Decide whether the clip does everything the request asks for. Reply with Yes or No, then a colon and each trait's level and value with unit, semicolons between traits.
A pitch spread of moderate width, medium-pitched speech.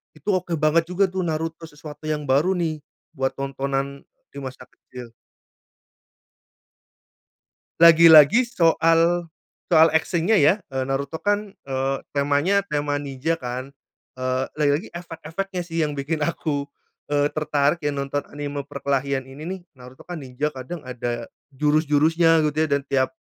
Yes: average, 3.1 semitones; medium, 150 Hz